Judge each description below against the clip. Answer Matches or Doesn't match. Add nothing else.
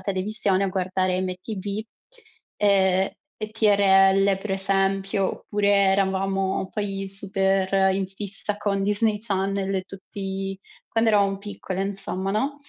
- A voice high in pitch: Matches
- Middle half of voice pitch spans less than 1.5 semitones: Matches